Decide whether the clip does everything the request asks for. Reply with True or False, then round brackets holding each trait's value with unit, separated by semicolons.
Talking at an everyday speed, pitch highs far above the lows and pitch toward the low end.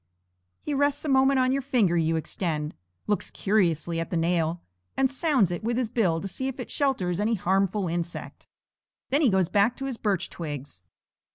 False (190 wpm; 7.4 semitones; 195 Hz)